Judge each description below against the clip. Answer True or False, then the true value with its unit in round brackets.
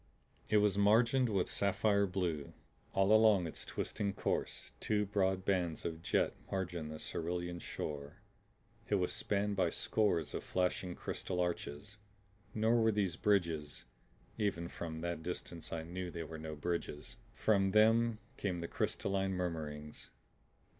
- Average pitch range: True (3.5 semitones)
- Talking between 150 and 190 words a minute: False (140 wpm)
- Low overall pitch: True (90 Hz)